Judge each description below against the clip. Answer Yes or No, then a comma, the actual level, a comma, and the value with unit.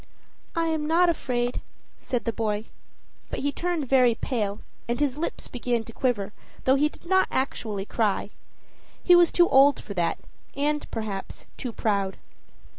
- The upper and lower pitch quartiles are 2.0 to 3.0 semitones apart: No, wide, 5.5 semitones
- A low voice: No, very high, 250 Hz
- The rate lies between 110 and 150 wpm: No, average, 160 wpm